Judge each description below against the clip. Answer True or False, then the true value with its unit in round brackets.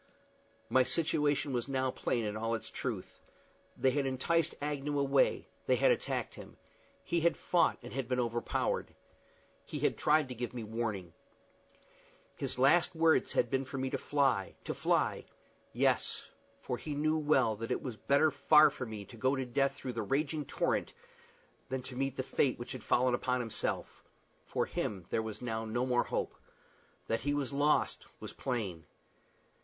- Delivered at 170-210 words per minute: True (175 wpm)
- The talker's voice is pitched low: True (130 Hz)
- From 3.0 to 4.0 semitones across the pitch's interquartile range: True (3.5 semitones)